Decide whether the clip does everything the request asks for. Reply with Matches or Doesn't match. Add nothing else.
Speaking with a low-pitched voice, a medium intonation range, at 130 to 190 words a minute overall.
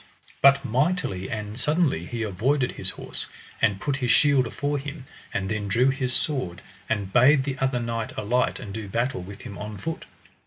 Matches